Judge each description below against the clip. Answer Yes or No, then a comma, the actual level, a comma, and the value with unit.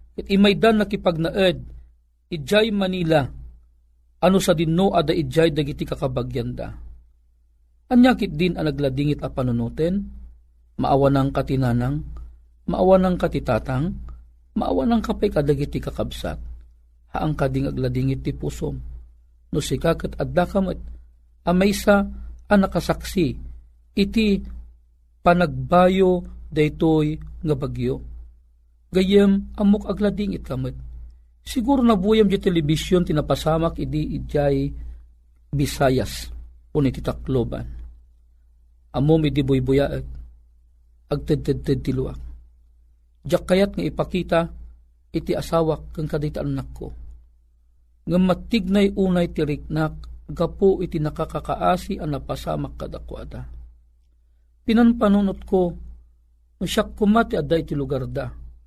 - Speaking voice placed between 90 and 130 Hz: No, medium, 140 Hz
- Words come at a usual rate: No, slow, 95 wpm